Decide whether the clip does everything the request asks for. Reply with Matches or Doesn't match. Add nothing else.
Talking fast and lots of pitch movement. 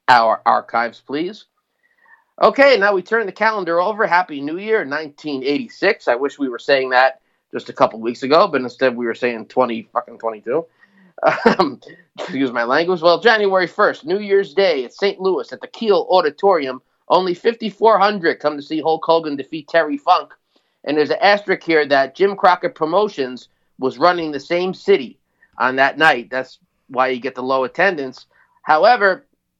Doesn't match